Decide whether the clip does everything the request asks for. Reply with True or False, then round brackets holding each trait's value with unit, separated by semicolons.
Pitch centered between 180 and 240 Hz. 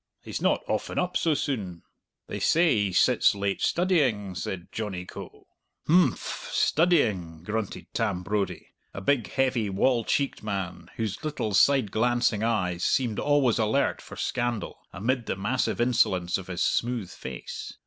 False (110 Hz)